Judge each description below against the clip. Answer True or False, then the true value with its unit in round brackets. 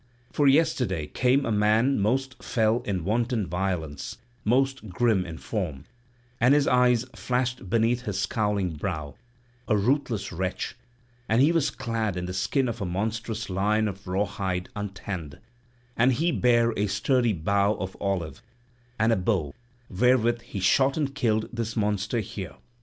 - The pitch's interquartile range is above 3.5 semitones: True (4.4 semitones)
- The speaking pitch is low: True (110 Hz)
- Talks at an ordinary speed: True (155 wpm)